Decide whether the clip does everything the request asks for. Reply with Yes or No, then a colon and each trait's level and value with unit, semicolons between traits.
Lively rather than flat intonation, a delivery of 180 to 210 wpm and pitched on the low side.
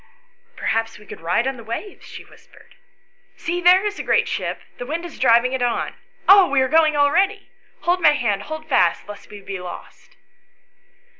No: wide, 7.5 semitones; average, 195 wpm; very high, 285 Hz